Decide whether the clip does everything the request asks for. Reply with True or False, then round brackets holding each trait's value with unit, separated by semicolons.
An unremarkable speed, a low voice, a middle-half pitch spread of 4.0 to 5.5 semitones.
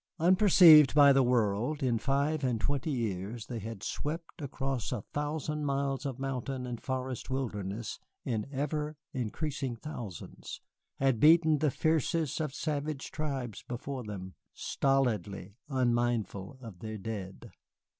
False (130 wpm; 130 Hz; 4.5 semitones)